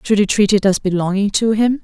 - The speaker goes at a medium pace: No, fast, 260 wpm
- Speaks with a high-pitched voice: Yes, high, 205 Hz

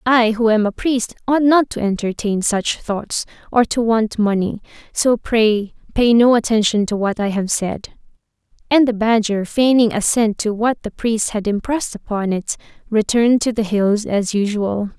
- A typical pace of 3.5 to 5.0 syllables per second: Yes, 4.5 syllables/s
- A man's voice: No, female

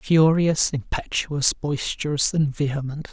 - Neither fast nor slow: No, slow, 95 wpm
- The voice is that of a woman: No, male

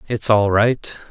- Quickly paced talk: No, average, 165 wpm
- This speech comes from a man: Yes, male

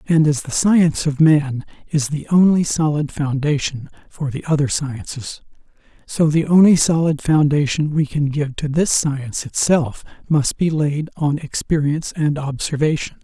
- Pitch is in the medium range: Yes, medium, 150 Hz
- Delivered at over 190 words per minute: No, average, 155 wpm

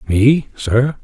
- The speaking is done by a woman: No, male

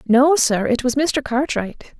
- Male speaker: No, female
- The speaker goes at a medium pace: Yes, average, 150 wpm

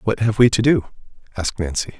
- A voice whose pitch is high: No, low, 110 Hz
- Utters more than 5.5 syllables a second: Yes, 6.2 syllables/s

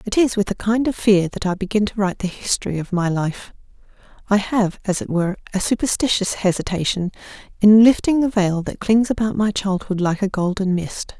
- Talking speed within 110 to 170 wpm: No, fast, 205 wpm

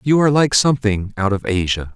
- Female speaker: No, male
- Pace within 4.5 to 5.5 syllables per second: No, 6.0 syllables/s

